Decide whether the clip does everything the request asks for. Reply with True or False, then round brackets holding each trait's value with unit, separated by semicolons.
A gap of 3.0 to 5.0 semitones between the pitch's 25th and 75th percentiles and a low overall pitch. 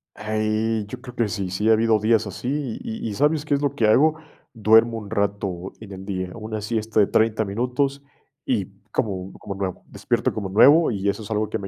False (2.6 semitones; 110 Hz)